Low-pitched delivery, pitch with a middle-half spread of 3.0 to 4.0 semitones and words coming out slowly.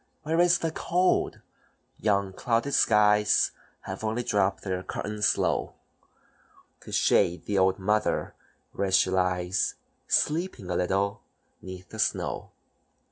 Yes: low, 105 Hz; average, 3.4 semitones; slow, 125 wpm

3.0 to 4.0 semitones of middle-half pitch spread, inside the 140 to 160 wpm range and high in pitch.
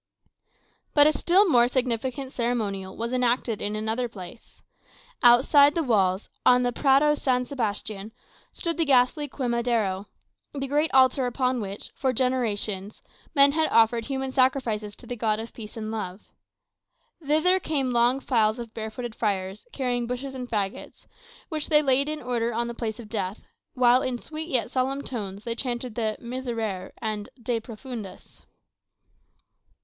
Yes: average, 3.3 semitones; average, 155 wpm; high, 240 Hz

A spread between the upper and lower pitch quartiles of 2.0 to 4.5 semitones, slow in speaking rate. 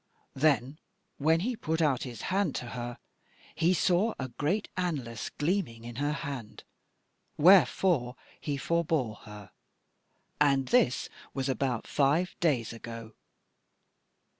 No: wide, 5.6 semitones; slow, 120 wpm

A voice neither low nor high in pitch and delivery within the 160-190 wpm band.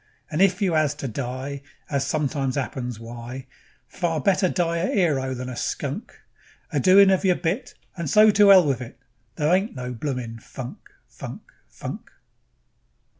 Yes: medium, 145 Hz; average, 170 wpm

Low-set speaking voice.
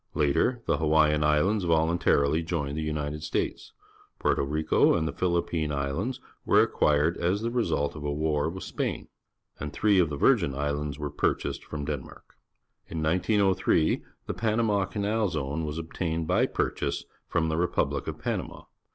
Yes: very low, 80 Hz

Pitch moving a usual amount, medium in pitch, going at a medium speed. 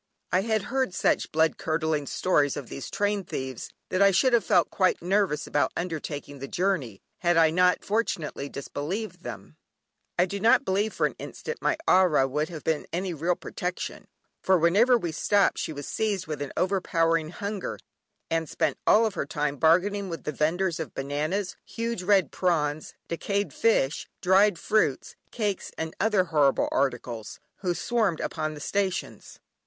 Yes: average, 4.6 semitones; medium, 175 Hz; average, 165 wpm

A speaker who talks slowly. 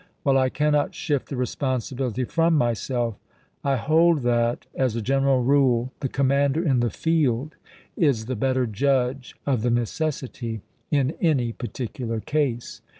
No: average, 145 wpm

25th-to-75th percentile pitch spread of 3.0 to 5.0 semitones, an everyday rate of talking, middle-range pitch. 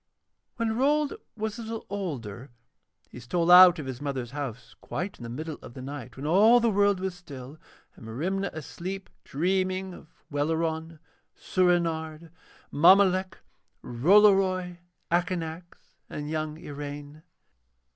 No: average, 4.7 semitones; slow, 130 wpm; medium, 170 Hz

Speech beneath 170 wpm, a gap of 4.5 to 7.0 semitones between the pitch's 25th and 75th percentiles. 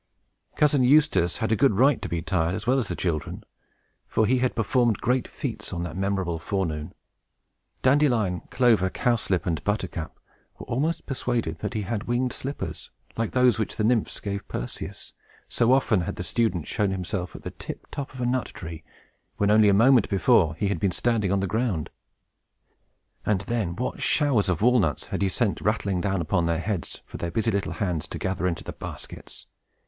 No: average, 190 wpm; average, 5.3 semitones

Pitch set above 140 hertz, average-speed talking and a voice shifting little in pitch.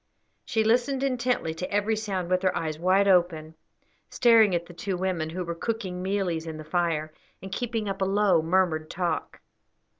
No: medium, 185 Hz; average, 180 wpm; average, 3.6 semitones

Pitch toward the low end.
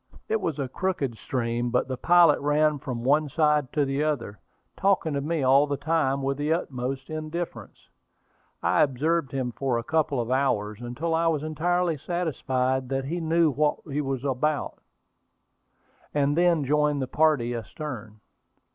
No: medium, 145 Hz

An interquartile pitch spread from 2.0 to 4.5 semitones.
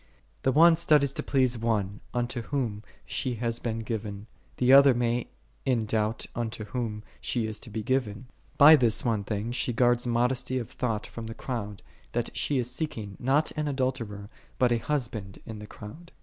Yes: average, 3.1 semitones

